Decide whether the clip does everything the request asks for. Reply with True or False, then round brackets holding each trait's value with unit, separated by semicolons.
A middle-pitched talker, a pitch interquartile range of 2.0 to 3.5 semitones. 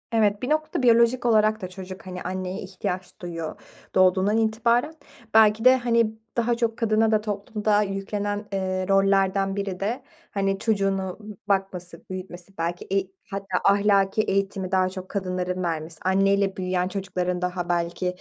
False (195 Hz; 2.6 semitones)